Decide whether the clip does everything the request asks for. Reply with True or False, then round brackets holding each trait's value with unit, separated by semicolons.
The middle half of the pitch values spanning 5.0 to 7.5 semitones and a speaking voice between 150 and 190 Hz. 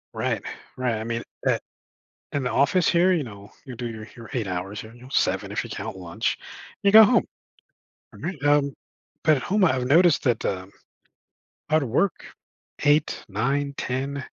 False (5.4 semitones; 130 Hz)